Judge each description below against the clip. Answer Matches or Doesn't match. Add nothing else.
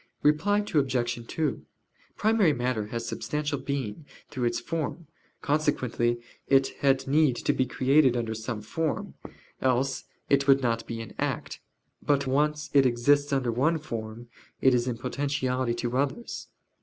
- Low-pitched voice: Matches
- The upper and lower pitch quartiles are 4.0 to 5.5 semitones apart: Doesn't match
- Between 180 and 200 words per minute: Doesn't match